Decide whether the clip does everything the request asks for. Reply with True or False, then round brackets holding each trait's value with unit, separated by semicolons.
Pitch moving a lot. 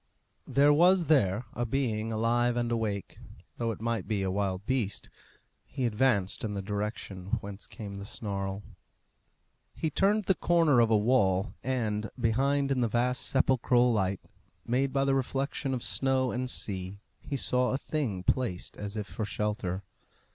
False (4.5 semitones)